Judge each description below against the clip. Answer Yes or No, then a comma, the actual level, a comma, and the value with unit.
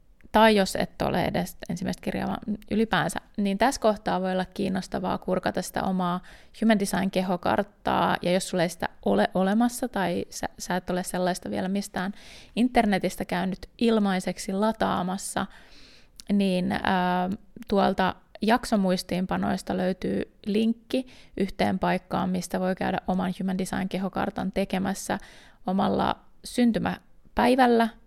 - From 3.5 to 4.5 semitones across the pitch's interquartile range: No, average, 2.9 semitones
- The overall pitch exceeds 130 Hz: Yes, high, 190 Hz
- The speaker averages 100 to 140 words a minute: Yes, average, 120 wpm